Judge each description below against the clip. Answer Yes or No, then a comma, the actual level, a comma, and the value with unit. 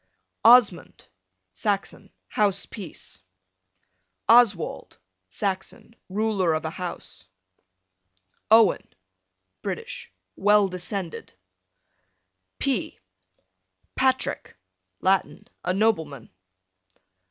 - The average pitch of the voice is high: Yes, high, 195 Hz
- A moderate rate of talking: No, slow, 65 wpm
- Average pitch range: Yes, average, 3.8 semitones